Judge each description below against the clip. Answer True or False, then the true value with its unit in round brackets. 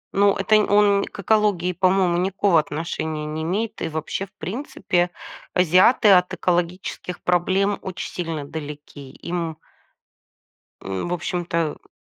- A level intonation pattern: False (3.3 semitones)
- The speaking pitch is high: False (180 Hz)